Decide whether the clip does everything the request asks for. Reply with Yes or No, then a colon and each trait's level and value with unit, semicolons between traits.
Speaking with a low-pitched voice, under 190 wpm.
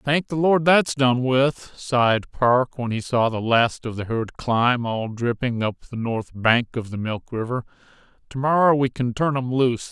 No: low, 125 Hz; fast, 205 wpm